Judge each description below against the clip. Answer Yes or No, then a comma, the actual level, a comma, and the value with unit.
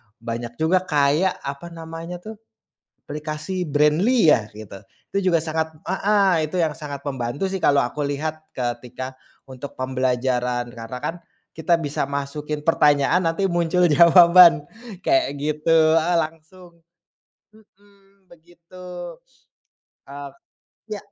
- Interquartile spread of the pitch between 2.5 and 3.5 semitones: No, average, 3.9 semitones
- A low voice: No, medium, 155 Hz